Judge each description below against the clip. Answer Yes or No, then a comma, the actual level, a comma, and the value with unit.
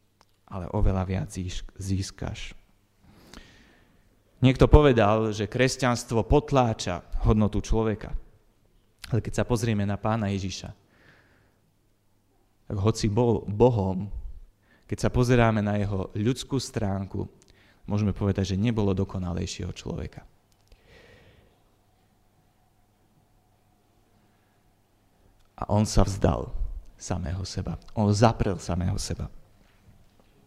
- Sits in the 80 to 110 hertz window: Yes, low, 100 Hz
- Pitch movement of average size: No, narrow, 2.2 semitones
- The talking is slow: Yes, slow, 90 wpm